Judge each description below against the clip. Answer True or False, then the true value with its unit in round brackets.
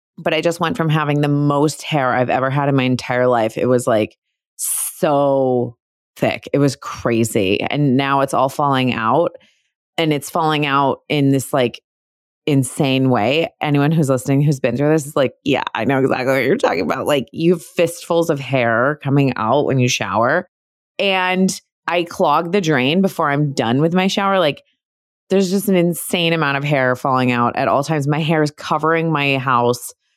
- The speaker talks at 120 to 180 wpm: False (195 wpm)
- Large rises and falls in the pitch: False (4.1 semitones)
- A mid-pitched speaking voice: True (145 Hz)